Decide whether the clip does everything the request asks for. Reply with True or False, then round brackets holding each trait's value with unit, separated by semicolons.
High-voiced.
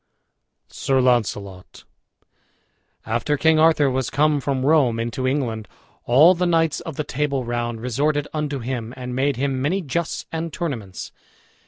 False (135 Hz)